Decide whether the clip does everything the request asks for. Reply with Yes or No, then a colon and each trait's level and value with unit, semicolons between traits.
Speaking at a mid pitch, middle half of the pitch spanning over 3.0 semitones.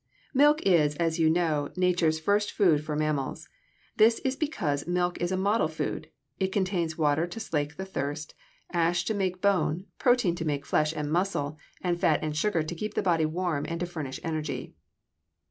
Yes: medium, 170 Hz; average, 3.6 semitones